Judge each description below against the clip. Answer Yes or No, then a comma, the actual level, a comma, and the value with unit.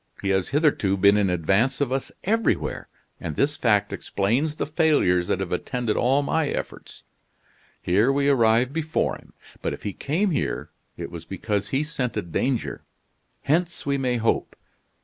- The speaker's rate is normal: Yes, average, 165 wpm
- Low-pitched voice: Yes, low, 125 Hz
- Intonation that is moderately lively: No, wide, 6.5 semitones